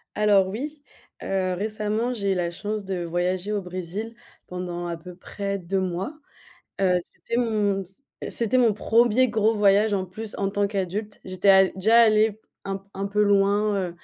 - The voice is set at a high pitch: Yes, high, 200 Hz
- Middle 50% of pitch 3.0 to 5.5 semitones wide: No, narrow, 2.4 semitones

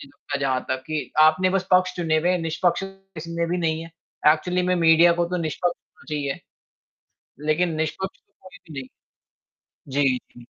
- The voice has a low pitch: No, medium, 165 Hz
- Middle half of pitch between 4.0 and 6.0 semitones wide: No, average, 2.7 semitones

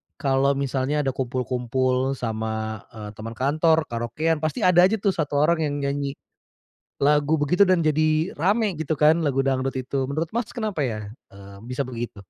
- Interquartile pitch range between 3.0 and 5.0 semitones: Yes, average, 3.8 semitones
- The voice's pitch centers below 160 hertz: Yes, medium, 140 Hz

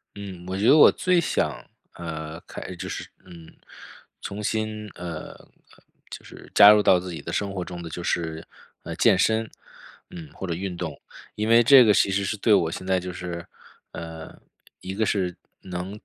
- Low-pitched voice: Yes, very low, 95 Hz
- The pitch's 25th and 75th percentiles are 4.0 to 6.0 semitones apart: No, average, 3.5 semitones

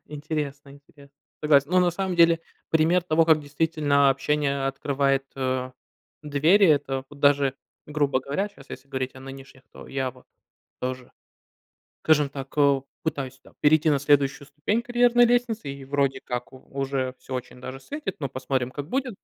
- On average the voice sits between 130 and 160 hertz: Yes, medium, 140 Hz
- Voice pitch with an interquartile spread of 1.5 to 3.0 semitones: Yes, average, 2.7 semitones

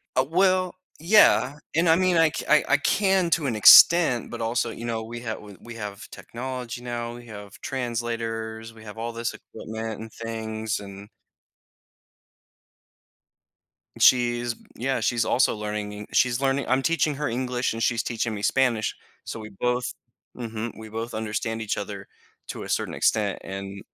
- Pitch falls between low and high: No, low, 115 Hz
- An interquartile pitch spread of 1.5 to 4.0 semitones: Yes, average, 2.9 semitones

